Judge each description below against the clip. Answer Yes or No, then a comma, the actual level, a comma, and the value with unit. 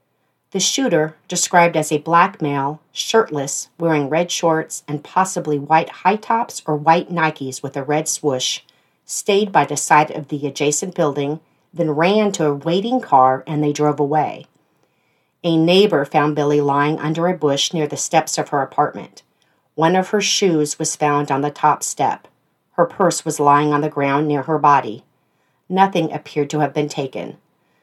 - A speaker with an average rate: Yes, average, 175 wpm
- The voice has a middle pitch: Yes, medium, 155 Hz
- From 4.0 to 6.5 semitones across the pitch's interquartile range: No, average, 2.8 semitones